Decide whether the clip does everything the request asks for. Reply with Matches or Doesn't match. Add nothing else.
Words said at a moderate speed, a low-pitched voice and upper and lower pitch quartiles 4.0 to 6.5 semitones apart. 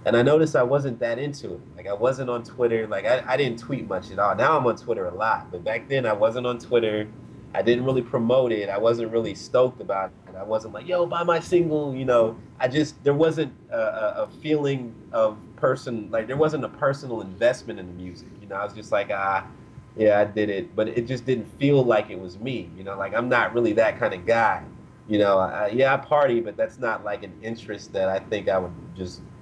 Doesn't match